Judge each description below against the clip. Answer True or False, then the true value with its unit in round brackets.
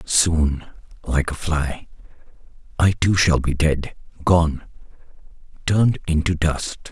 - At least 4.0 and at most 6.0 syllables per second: False (3.6 syllables/s)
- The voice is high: False (80 Hz)